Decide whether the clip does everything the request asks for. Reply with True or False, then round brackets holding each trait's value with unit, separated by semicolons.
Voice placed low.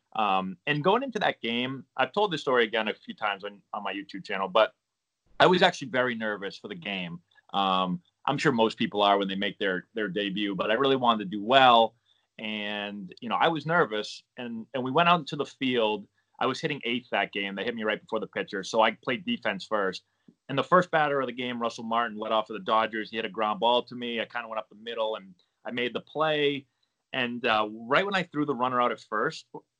True (115 Hz)